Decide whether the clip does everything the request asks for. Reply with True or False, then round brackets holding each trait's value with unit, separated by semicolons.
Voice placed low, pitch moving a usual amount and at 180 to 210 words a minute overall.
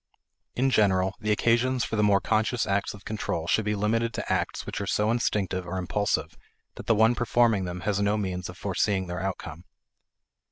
True (105 Hz; 3.0 semitones; 195 wpm)